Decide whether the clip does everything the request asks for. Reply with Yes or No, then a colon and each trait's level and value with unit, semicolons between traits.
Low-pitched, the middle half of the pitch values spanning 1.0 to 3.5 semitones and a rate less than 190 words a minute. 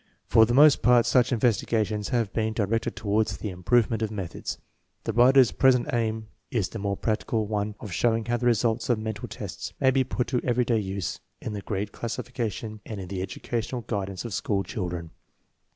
No: low, 110 Hz; average, 2.8 semitones; average, 195 wpm